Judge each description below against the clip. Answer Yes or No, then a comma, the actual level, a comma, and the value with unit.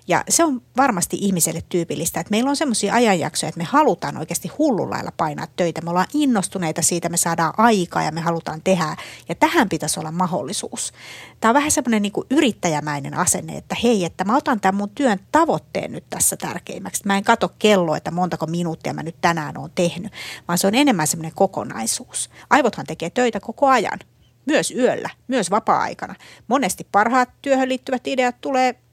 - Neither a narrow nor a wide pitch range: No, wide, 6.7 semitones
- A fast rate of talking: Yes, fast, 180 wpm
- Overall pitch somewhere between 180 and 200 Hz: Yes, high, 190 Hz